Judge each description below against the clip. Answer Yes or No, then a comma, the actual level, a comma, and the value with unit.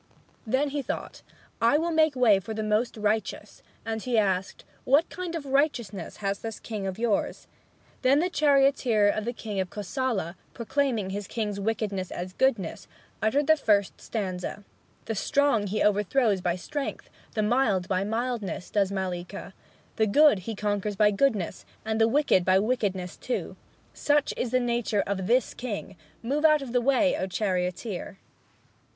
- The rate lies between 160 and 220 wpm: Yes, average, 165 wpm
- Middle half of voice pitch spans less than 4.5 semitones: No, average, 4.8 semitones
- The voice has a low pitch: No, high, 220 Hz